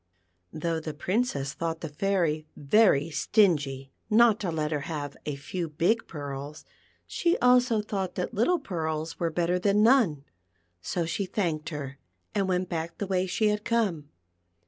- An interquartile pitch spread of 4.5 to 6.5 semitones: Yes, average, 5.2 semitones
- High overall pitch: No, medium, 170 Hz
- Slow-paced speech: No, average, 160 wpm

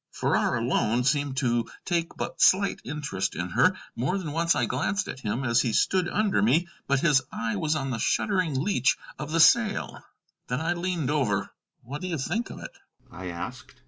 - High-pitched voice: No, medium, 145 Hz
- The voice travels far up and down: Yes, wide, 6.3 semitones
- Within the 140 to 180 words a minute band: No, average, 195 wpm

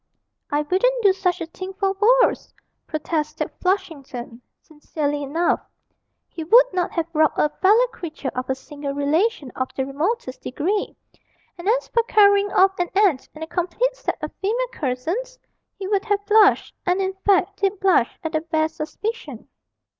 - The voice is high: Yes, very high, 360 Hz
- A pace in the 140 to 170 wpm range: Yes, average, 165 wpm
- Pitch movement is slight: No, average, 5.3 semitones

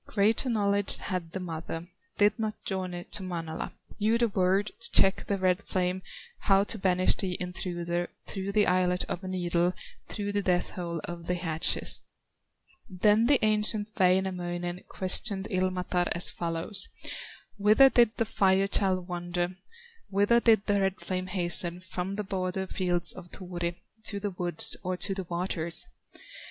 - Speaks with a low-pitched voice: No, medium, 185 Hz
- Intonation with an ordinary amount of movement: No, narrow, 2.3 semitones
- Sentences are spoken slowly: No, average, 155 wpm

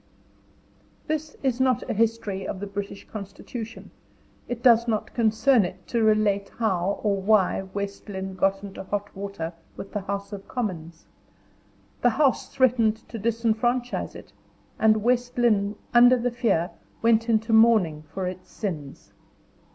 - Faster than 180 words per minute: No, average, 150 wpm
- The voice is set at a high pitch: Yes, high, 215 Hz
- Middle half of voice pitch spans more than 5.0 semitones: No, average, 3.1 semitones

